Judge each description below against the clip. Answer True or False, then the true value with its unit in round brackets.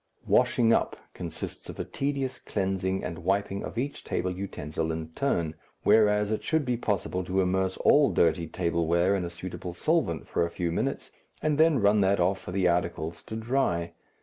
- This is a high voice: False (95 Hz)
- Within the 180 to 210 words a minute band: True (185 wpm)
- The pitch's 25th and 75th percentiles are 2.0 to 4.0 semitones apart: False (4.4 semitones)